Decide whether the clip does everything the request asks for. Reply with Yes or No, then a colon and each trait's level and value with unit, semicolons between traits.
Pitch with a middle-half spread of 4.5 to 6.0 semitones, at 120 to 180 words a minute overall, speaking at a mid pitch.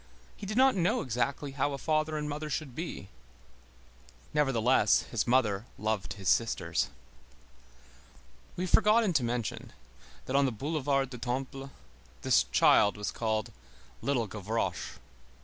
No: average, 5.1 semitones; slow, 135 wpm; low, 130 Hz